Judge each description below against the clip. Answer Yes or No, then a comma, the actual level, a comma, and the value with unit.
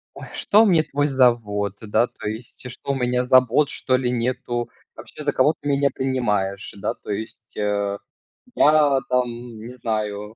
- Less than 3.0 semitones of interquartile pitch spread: No, average, 3.8 semitones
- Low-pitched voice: Yes, low, 125 Hz